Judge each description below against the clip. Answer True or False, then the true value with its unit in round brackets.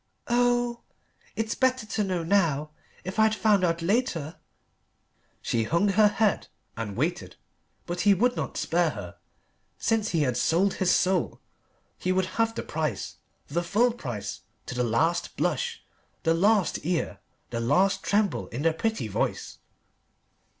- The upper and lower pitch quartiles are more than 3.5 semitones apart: True (5.2 semitones)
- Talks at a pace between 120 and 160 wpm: True (150 wpm)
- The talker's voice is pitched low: False (185 Hz)